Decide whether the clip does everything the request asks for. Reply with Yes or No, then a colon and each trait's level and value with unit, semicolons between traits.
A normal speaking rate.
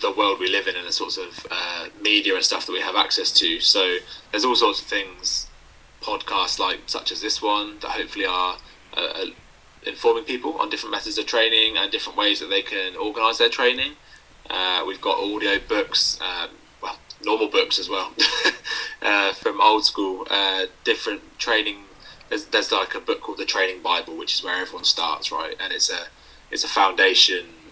Yes: average, 195 wpm